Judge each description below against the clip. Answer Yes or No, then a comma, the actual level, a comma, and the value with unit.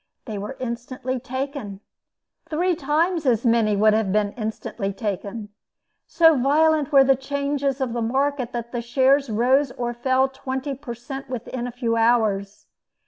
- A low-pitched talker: No, very high, 255 Hz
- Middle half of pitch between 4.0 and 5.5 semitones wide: No, average, 3.2 semitones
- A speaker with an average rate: Yes, average, 150 wpm